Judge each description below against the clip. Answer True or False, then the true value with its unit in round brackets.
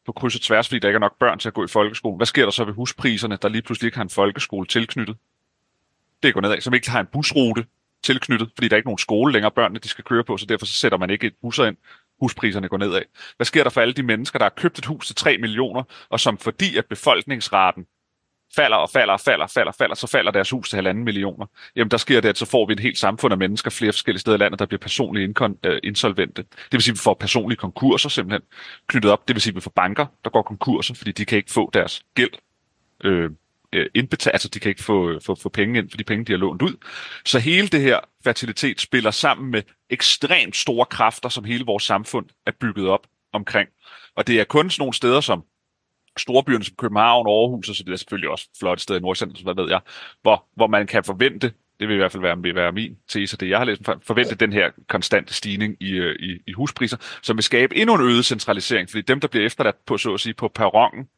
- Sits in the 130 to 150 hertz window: False (110 Hz)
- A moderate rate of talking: False (255 wpm)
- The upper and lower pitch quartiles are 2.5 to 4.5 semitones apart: True (3.5 semitones)